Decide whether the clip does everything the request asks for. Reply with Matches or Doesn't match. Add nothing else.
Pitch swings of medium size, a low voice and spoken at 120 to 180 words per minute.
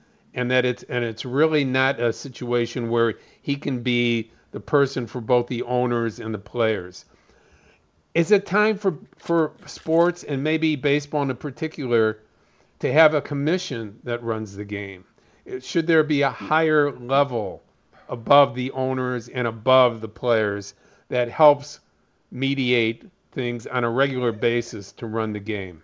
Matches